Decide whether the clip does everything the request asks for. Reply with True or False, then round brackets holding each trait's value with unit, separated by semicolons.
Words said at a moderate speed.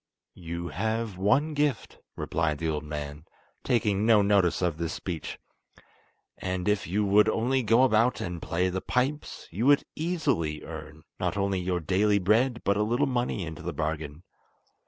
True (165 wpm)